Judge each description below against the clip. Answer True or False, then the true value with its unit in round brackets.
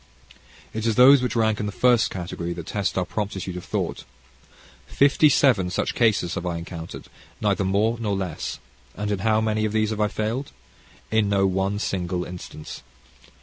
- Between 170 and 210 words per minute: True (180 wpm)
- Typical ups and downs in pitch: True (3.2 semitones)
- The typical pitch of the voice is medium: False (105 Hz)